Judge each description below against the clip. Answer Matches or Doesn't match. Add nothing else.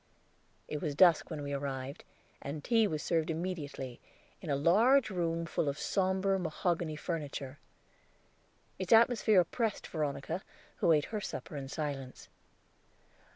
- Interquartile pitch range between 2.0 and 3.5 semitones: Doesn't match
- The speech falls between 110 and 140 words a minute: Matches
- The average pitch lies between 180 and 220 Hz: Doesn't match